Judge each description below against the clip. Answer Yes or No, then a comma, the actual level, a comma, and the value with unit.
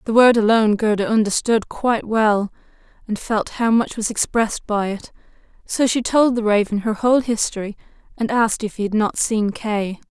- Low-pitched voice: No, high, 220 Hz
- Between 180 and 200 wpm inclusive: Yes, average, 185 wpm